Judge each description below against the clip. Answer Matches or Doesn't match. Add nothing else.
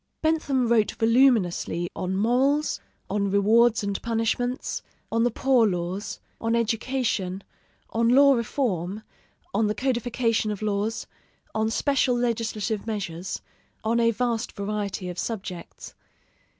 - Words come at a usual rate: Doesn't match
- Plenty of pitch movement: Doesn't match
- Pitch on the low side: Doesn't match